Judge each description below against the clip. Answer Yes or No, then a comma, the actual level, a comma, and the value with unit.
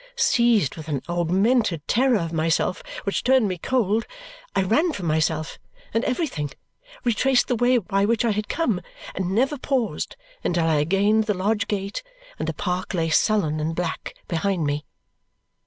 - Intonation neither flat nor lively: No, wide, 6.1 semitones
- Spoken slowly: No, average, 170 wpm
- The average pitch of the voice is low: No, high, 200 Hz